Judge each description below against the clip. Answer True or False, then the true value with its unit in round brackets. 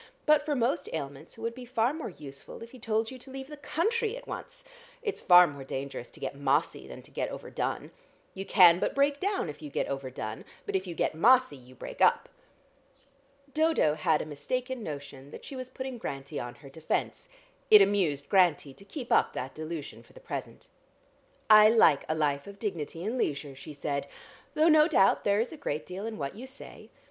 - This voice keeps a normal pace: False (215 wpm)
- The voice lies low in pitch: False (195 Hz)